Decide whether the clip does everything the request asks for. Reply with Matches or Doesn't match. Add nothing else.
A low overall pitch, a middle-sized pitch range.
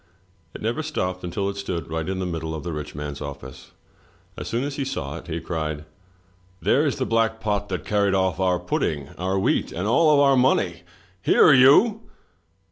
Doesn't match